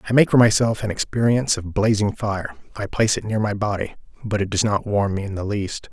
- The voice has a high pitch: No, low, 105 Hz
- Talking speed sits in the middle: No, fast, 245 wpm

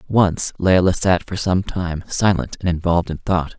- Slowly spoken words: No, average, 185 wpm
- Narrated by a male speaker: Yes, male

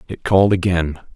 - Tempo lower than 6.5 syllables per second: Yes, 5.7 syllables/s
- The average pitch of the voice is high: No, very low, 90 Hz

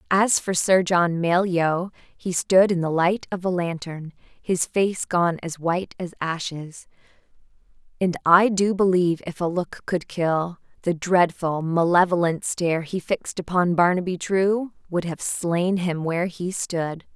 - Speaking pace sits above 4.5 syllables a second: No, 4.1 syllables/s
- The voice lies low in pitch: No, medium, 175 Hz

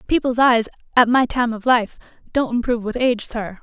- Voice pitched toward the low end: No, high, 240 Hz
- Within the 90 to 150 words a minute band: No, average, 200 wpm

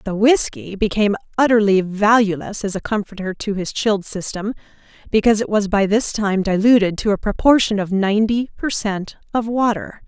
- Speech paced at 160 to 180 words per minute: Yes, average, 165 wpm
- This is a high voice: Yes, high, 210 Hz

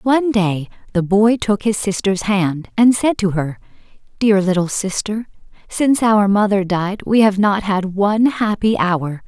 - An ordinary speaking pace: Yes, average, 170 wpm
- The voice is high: Yes, high, 200 Hz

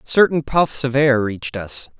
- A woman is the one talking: No, male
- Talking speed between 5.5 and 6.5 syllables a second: No, 4.4 syllables/s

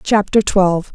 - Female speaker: Yes, female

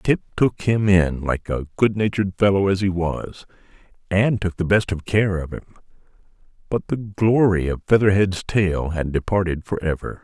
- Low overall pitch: Yes, very low, 95 Hz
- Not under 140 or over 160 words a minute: No, average, 170 wpm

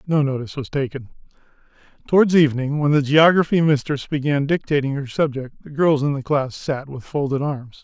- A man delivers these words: Yes, male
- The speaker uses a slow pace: No, average, 175 wpm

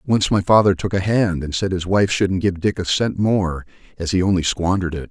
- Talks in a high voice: No, very low, 95 Hz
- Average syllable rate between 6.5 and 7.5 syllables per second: No, 5.4 syllables/s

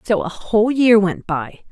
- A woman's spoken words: Yes, female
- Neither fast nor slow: No, fast, 210 wpm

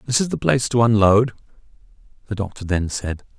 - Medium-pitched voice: No, low, 110 Hz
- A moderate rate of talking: Yes, average, 175 wpm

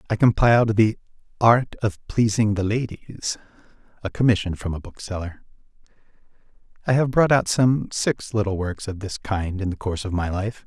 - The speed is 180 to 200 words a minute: No, average, 170 wpm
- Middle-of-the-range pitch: No, low, 105 Hz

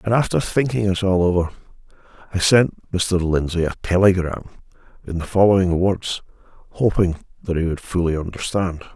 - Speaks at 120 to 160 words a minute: Yes, average, 145 wpm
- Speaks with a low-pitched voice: Yes, very low, 90 Hz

